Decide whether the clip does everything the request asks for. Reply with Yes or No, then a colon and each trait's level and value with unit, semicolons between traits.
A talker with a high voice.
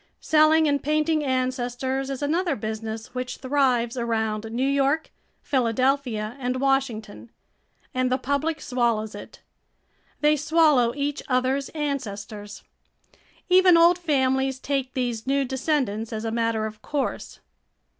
Yes: very high, 260 Hz